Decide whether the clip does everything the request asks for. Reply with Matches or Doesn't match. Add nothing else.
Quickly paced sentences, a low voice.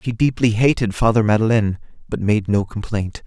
Doesn't match